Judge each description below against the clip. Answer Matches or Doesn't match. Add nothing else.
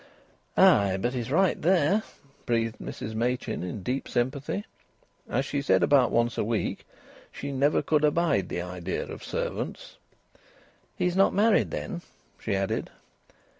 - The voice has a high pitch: Doesn't match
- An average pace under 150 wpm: Matches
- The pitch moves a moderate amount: Doesn't match